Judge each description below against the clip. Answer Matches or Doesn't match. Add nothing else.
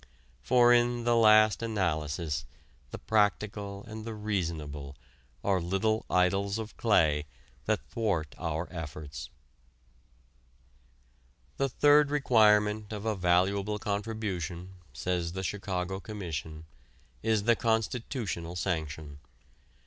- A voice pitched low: Matches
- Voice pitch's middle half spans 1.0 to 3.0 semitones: Doesn't match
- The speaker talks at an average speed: Doesn't match